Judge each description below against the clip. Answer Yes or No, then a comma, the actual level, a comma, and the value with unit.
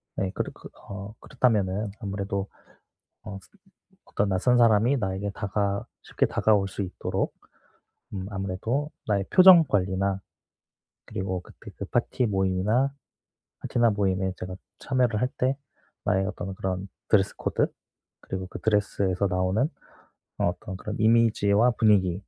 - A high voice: No, low, 100 Hz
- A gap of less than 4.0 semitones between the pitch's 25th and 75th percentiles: Yes, average, 2.7 semitones